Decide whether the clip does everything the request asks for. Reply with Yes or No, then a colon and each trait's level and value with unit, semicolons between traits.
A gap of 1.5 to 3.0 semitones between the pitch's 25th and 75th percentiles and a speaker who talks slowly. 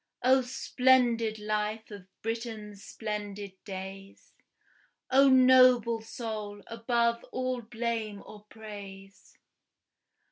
Yes: narrow, 2.6 semitones; slow, 85 wpm